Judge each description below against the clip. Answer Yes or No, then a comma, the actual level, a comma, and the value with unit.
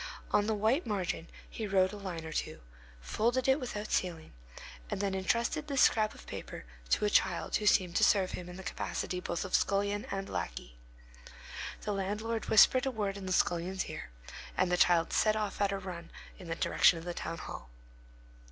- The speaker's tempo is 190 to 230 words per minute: Yes, average, 200 wpm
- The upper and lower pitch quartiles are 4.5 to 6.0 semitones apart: No, average, 3.2 semitones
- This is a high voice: Yes, high, 195 Hz